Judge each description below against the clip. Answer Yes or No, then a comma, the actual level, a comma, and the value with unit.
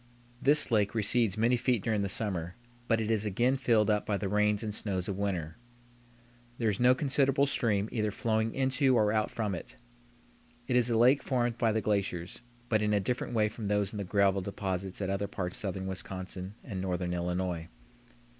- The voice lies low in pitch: Yes, low, 105 Hz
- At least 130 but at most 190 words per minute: No, average, 200 wpm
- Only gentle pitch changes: No, average, 3.3 semitones